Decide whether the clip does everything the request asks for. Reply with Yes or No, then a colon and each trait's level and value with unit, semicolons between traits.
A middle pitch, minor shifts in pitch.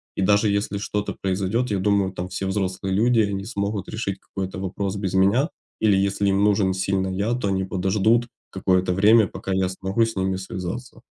No: very low, 95 Hz; narrow, 1.6 semitones